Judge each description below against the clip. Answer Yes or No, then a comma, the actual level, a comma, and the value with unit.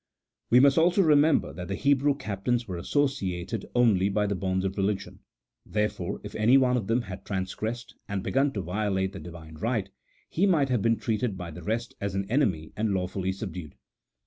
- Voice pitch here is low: Yes, low, 105 Hz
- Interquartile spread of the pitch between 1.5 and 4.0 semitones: No, average, 4.7 semitones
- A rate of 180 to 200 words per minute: Yes, average, 190 wpm